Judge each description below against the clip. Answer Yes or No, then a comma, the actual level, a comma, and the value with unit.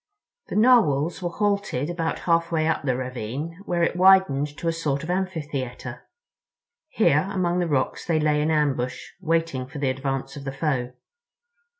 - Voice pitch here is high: No, medium, 155 Hz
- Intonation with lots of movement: No, average, 4.2 semitones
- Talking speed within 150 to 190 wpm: Yes, average, 165 wpm